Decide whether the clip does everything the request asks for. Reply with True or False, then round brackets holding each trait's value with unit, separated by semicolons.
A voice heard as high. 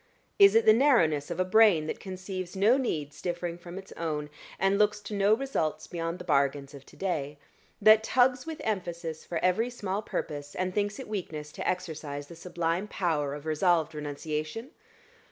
False (175 Hz)